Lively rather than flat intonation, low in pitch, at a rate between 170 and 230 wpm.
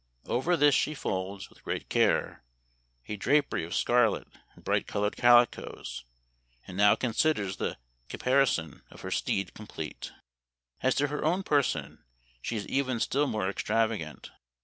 No: wide, 6.0 semitones; low, 115 Hz; average, 150 wpm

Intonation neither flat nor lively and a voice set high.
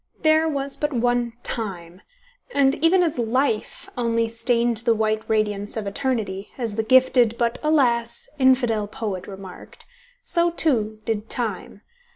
Yes: average, 3.3 semitones; high, 235 Hz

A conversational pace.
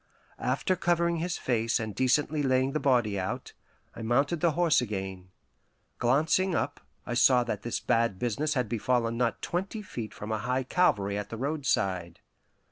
Yes: average, 165 wpm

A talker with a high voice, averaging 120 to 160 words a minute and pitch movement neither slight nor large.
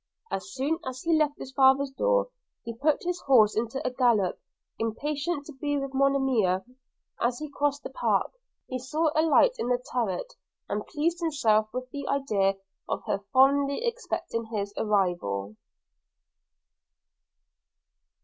Yes: very high, 265 Hz; average, 150 wpm; average, 4.9 semitones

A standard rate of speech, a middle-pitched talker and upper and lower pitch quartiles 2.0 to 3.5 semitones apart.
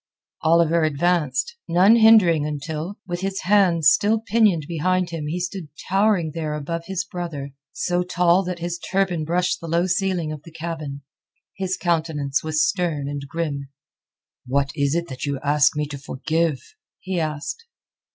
Yes: average, 160 wpm; medium, 170 Hz; average, 3.2 semitones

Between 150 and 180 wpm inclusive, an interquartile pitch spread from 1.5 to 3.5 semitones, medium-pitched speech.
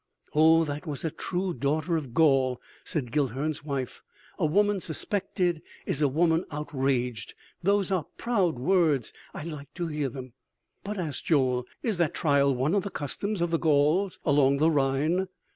No: average, 165 wpm; average, 3.9 semitones; medium, 155 Hz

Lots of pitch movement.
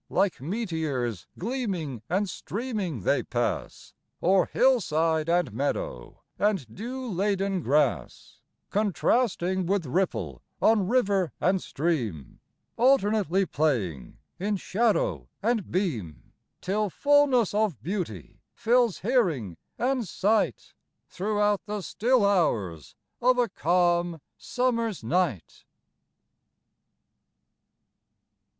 Yes: wide, 6.2 semitones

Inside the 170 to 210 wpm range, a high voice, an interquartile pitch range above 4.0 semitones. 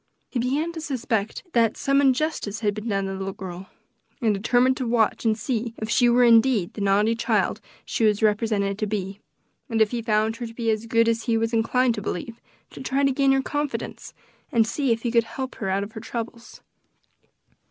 No: fast, 205 wpm; high, 230 Hz; average, 2.8 semitones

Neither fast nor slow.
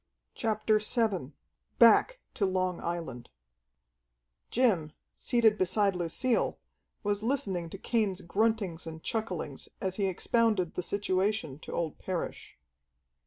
No: slow, 115 wpm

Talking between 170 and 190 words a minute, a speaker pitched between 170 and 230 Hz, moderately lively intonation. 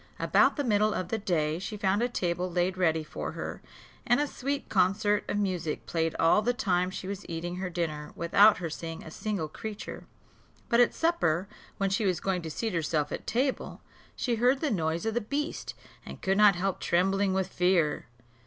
No: average, 200 wpm; high, 190 Hz; average, 4.0 semitones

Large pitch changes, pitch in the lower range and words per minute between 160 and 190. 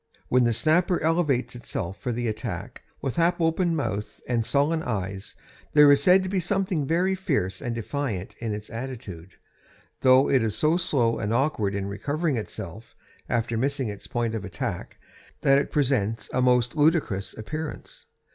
Yes: wide, 5.7 semitones; low, 125 Hz; average, 165 wpm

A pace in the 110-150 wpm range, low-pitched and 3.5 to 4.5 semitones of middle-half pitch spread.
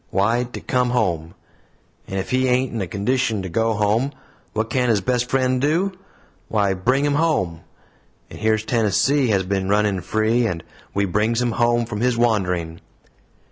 No: average, 175 wpm; low, 110 Hz; average, 4.0 semitones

